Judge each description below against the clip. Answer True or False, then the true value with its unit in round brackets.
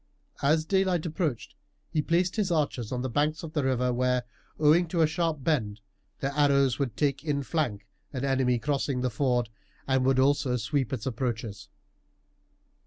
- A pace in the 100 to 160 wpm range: False (170 wpm)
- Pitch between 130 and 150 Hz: True (140 Hz)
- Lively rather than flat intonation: False (3.6 semitones)